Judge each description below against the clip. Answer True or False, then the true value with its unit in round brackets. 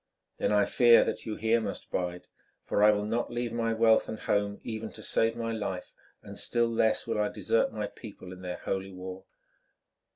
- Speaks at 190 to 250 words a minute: True (200 wpm)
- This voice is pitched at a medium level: False (110 Hz)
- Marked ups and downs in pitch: False (2.6 semitones)